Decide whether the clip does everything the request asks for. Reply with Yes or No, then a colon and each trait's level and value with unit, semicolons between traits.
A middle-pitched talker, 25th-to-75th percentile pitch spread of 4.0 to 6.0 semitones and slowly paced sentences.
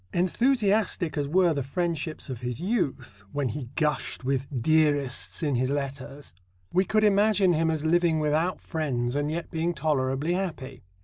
No: medium, 155 Hz; average, 4.3 semitones; average, 160 wpm